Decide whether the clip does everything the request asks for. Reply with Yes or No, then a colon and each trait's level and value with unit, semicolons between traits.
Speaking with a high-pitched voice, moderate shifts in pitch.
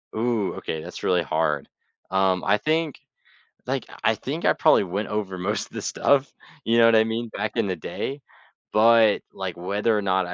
No: low, 105 Hz; average, 3.6 semitones